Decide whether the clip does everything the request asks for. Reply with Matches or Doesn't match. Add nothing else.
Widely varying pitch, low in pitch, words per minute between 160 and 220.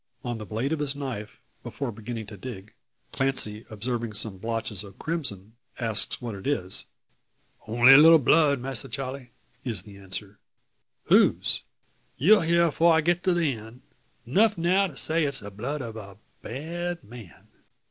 Matches